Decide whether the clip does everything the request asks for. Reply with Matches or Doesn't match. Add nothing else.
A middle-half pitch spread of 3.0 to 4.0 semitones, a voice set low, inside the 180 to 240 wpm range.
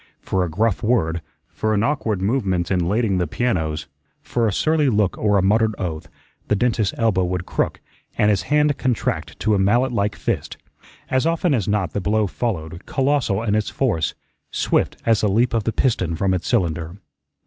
Doesn't match